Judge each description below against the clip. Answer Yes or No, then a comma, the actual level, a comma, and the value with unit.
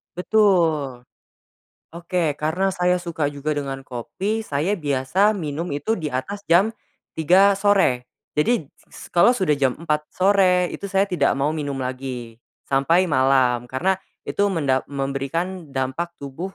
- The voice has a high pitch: No, medium, 155 Hz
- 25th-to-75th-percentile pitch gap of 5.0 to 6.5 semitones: Yes, average, 5.3 semitones